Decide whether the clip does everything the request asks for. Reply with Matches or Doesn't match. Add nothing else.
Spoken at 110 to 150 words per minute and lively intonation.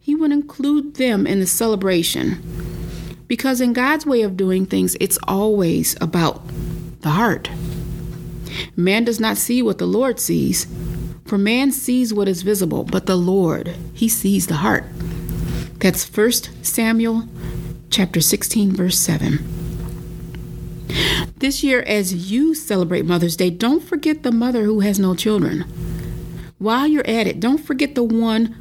Matches